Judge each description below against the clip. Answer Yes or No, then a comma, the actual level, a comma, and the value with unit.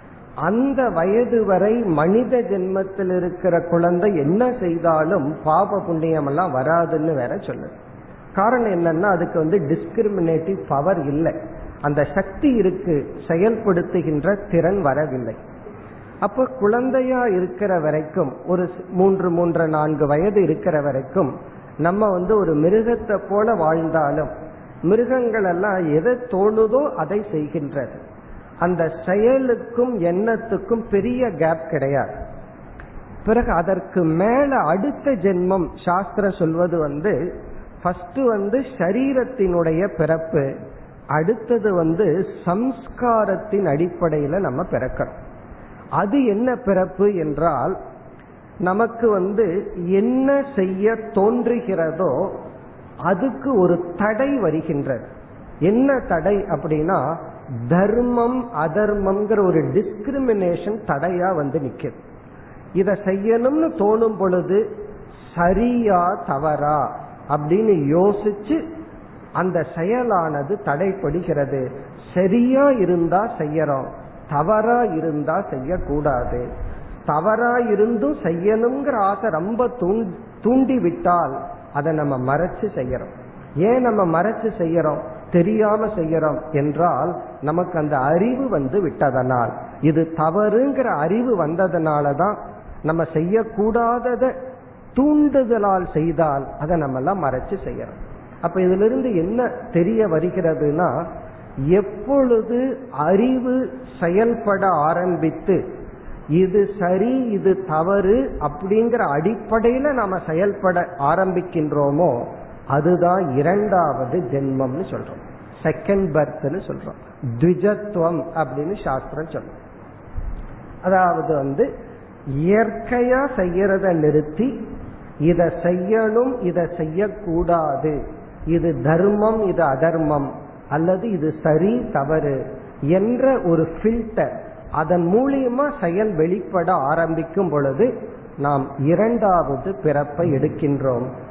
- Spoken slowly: No, average, 85 wpm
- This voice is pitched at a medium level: Yes, medium, 180 Hz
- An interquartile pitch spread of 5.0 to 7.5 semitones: Yes, wide, 5.4 semitones